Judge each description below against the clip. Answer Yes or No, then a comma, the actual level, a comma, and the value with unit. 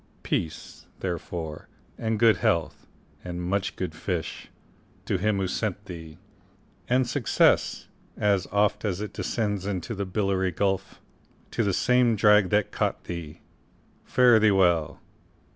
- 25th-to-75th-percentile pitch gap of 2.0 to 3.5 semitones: Yes, average, 3.1 semitones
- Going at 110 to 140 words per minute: Yes, slow, 135 wpm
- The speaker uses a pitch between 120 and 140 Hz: No, low, 100 Hz